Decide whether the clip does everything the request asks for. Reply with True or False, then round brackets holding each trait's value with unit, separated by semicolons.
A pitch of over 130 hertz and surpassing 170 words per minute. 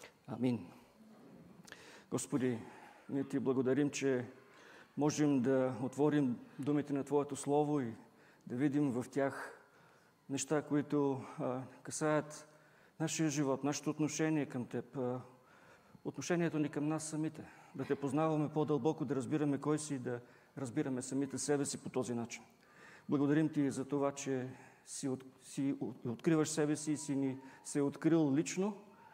False (140 Hz; 140 wpm)